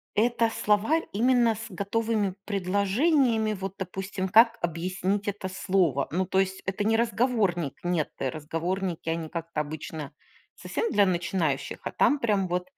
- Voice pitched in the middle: No, high, 195 Hz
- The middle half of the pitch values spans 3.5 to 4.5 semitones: Yes, average, 4.0 semitones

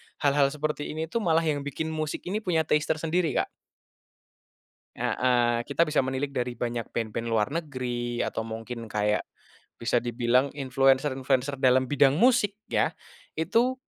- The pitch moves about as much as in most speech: Yes, average, 4.4 semitones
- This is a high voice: No, low, 135 Hz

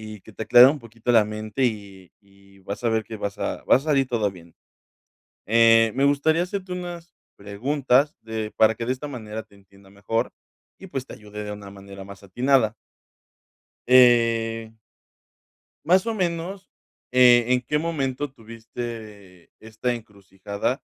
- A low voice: Yes, low, 115 Hz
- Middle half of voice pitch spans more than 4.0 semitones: Yes, average, 4.5 semitones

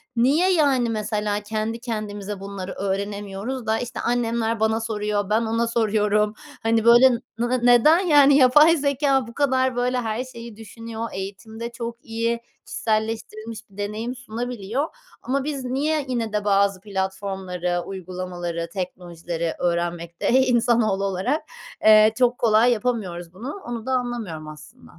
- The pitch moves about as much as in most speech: Yes, average, 3.5 semitones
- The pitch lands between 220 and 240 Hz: Yes, high, 225 Hz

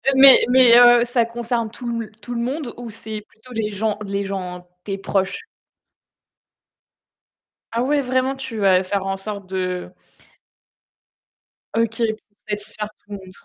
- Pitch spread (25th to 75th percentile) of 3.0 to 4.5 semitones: Yes, average, 3.5 semitones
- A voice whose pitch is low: No, high, 220 Hz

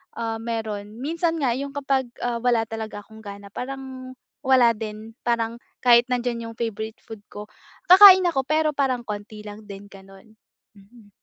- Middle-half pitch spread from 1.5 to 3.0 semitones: No, average, 3.5 semitones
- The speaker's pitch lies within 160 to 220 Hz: No, high, 230 Hz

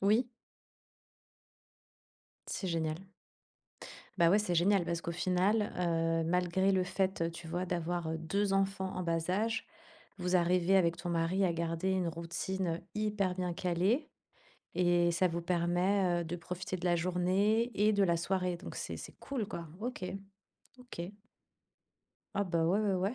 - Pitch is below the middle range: No, medium, 180 Hz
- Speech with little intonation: Yes, narrow, 2.3 semitones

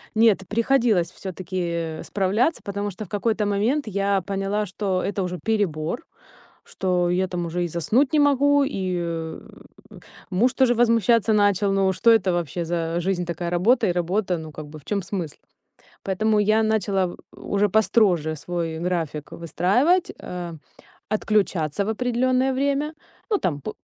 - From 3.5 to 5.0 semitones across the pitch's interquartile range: Yes, average, 4.1 semitones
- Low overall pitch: No, high, 195 Hz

